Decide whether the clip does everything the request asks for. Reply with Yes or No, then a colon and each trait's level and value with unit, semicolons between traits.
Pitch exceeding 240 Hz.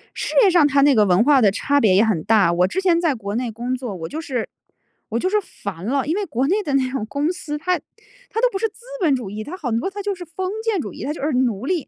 Yes: very high, 275 Hz